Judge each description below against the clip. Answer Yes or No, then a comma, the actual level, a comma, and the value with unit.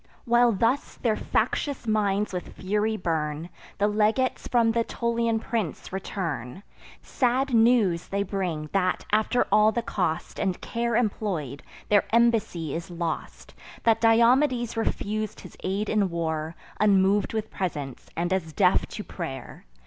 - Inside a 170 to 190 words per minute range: No, average, 140 wpm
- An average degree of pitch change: Yes, average, 4.7 semitones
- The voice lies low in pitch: No, high, 205 Hz